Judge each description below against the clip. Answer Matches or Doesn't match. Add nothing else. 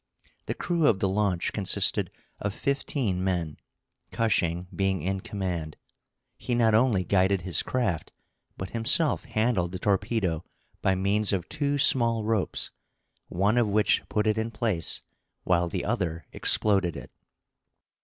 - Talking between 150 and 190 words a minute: Doesn't match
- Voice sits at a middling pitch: Doesn't match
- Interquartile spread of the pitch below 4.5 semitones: Matches